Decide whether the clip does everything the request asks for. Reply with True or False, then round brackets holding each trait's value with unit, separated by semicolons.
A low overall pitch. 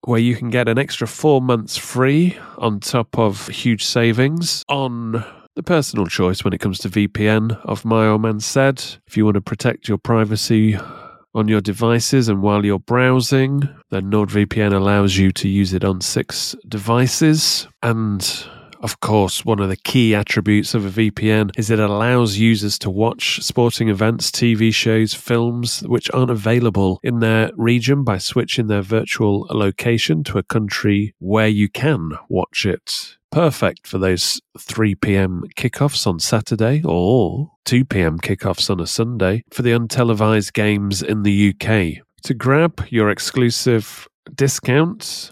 True (110 Hz)